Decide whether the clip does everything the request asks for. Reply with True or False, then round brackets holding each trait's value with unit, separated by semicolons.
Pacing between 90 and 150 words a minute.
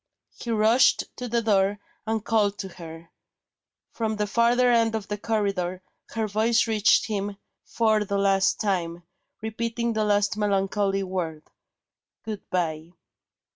True (135 wpm)